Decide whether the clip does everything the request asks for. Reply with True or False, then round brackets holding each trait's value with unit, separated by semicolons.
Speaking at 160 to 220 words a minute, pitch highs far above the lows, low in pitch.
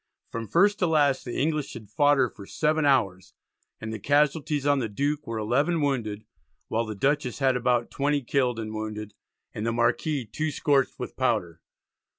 False (180 wpm; 4.7 semitones; 130 Hz)